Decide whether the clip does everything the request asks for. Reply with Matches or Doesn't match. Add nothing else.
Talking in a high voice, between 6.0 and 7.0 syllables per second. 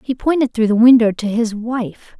Doesn't match